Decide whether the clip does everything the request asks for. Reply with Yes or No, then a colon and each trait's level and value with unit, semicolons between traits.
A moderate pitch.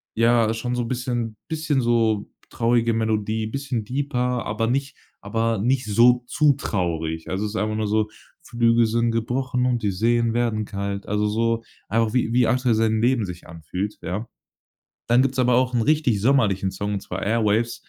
No: low, 115 Hz